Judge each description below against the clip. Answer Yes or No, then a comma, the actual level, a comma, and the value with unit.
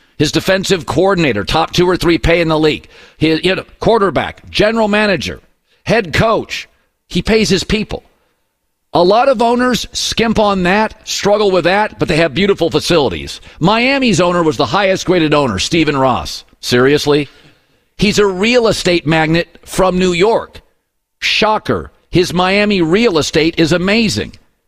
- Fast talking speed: No, average, 155 wpm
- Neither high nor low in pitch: Yes, medium, 180 Hz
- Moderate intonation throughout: Yes, average, 4.5 semitones